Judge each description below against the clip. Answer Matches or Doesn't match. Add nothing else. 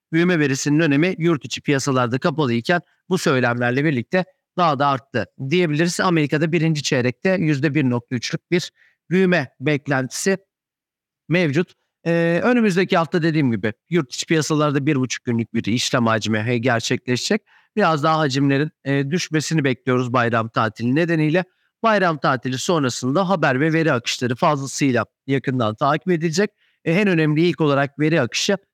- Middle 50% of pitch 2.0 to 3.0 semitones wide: Doesn't match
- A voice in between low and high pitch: Matches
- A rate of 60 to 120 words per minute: Doesn't match